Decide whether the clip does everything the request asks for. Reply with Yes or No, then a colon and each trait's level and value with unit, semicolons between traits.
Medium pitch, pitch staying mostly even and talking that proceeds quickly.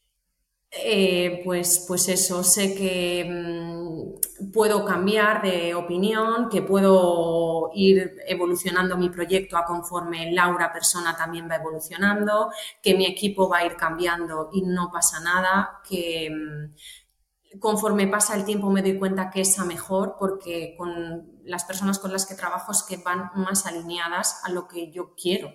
No: medium, 180 Hz; narrow, 2.1 semitones; average, 155 wpm